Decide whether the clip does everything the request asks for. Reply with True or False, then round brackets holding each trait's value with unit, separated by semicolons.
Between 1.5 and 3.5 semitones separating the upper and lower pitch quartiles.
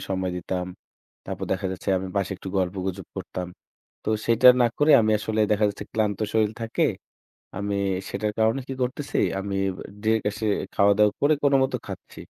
True (2.7 semitones)